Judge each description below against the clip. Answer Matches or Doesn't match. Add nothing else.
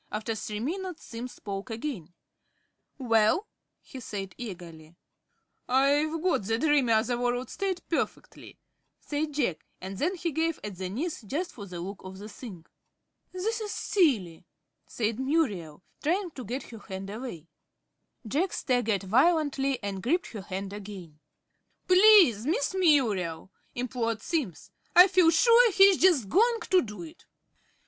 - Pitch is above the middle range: Matches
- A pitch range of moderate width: Doesn't match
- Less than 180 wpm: Matches